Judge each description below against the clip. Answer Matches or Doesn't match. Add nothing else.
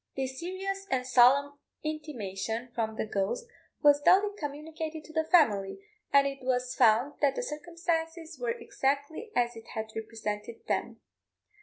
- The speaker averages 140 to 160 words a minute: Matches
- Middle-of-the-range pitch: Doesn't match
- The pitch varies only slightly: Doesn't match